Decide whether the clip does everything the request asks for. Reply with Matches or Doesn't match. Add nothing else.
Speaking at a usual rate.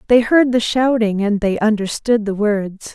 Matches